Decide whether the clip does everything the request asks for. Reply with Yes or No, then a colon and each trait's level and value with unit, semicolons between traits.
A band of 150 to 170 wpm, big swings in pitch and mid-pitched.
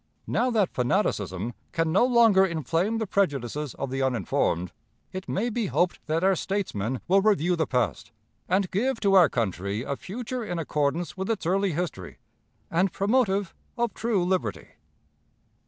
Yes: average, 155 wpm; wide, 6.7 semitones; medium, 180 Hz